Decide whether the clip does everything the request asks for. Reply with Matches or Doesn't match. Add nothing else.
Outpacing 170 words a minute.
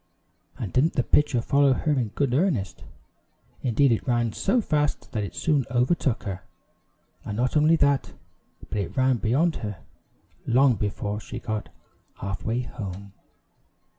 Doesn't match